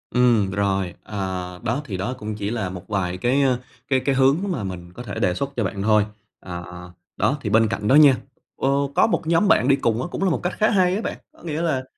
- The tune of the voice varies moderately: No, wide, 6.1 semitones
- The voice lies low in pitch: Yes, low, 115 Hz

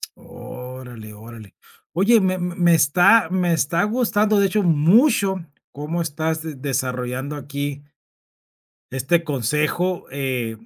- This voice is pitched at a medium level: Yes, medium, 155 Hz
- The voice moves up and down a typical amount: No, wide, 5.7 semitones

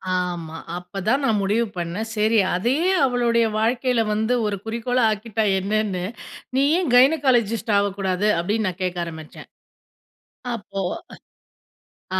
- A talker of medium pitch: No, high, 215 Hz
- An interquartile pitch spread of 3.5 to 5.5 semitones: Yes, average, 4.1 semitones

